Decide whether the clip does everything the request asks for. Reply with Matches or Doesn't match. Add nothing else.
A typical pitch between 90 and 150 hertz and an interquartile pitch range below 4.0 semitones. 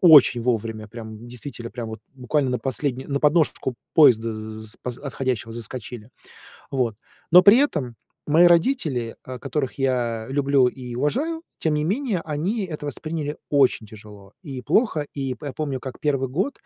Doesn't match